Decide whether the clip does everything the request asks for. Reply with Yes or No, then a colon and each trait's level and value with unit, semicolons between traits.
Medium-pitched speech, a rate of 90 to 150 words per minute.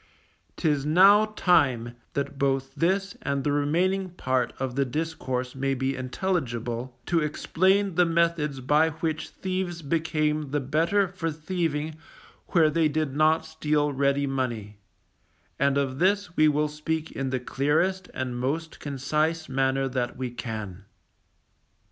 Yes: medium, 150 Hz; average, 140 wpm